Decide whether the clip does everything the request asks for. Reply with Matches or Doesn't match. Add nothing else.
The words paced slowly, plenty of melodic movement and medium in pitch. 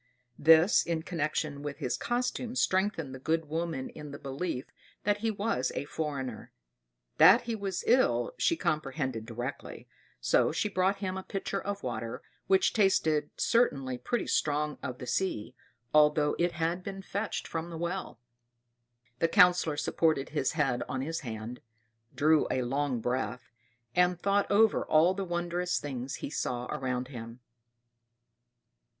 Doesn't match